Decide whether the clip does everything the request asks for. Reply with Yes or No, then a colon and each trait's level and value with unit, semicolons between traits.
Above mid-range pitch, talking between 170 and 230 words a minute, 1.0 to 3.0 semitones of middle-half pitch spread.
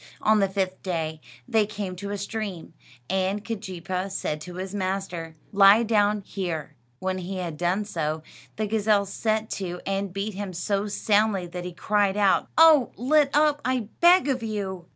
Yes: high, 195 Hz; average, 175 wpm; average, 2.7 semitones